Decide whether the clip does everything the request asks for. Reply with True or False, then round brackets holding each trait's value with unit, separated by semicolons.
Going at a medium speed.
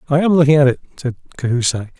False (210 wpm)